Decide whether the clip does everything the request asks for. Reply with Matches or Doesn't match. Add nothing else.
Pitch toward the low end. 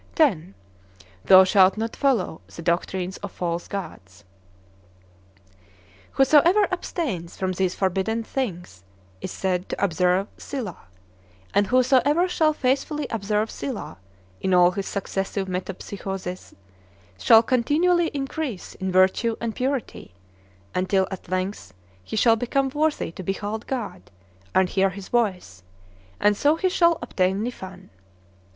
Doesn't match